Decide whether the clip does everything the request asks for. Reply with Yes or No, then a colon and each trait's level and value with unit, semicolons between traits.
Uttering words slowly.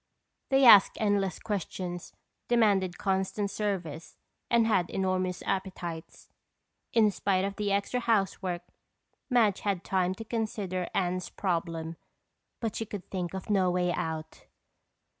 Yes: slow, 125 wpm